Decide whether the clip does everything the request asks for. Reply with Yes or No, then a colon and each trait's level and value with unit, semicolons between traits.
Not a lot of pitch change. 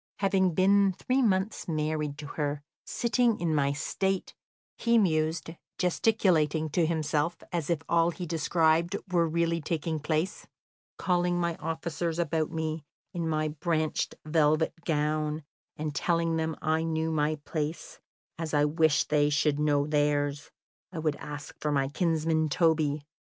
Yes: narrow, 2.1 semitones